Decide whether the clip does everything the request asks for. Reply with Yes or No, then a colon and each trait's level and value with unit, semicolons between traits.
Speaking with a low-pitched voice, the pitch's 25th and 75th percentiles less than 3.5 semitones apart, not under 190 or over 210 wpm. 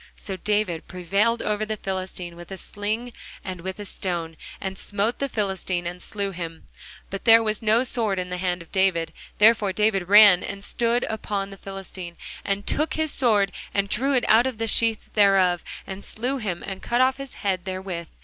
No: high, 200 Hz; average, 3.0 semitones; average, 195 wpm